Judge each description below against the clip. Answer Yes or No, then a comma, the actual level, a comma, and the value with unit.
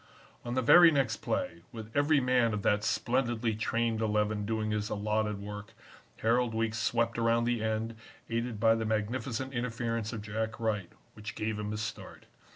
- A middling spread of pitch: No, narrow, 1.7 semitones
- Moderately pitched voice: No, low, 110 Hz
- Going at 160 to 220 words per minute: Yes, average, 170 wpm